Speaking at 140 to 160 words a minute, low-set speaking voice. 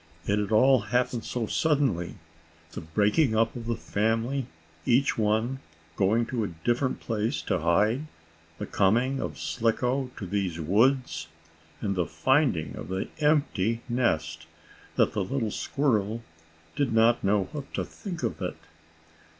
Yes: average, 145 wpm; low, 115 Hz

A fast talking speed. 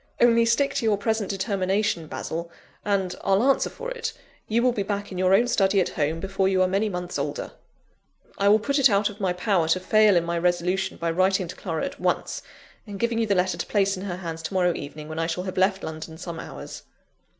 Yes: fast, 235 wpm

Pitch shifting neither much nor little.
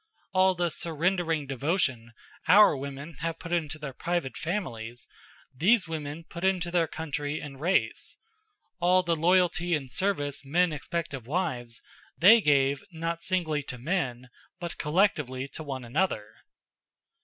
Yes: average, 4.4 semitones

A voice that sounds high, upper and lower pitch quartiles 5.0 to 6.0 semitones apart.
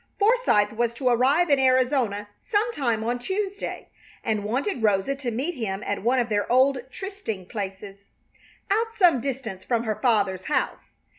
Yes: high, 245 Hz; wide, 5.5 semitones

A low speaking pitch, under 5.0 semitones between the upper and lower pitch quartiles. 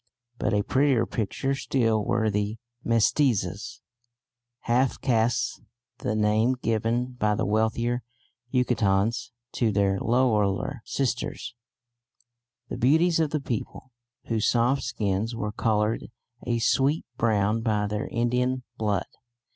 Yes: low, 115 Hz; average, 2.9 semitones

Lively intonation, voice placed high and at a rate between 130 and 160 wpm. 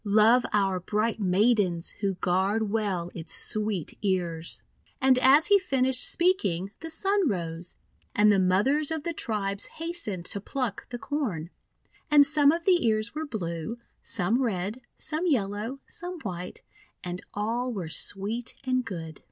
Yes: wide, 6.3 semitones; high, 215 Hz; average, 150 wpm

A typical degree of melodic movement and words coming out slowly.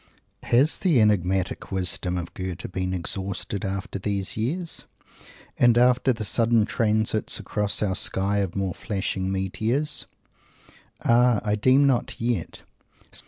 Yes: average, 3.9 semitones; slow, 130 wpm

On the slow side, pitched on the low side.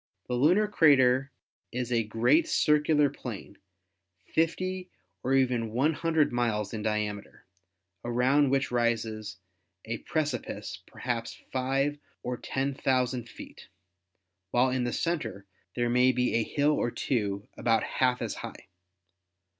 Yes: slow, 130 wpm; low, 125 Hz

